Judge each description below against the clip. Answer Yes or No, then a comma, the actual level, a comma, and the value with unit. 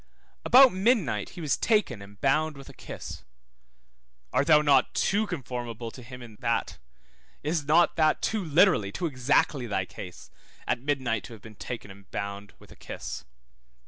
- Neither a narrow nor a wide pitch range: No, wide, 5.9 semitones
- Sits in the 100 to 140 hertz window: Yes, low, 135 Hz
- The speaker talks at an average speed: Yes, average, 170 wpm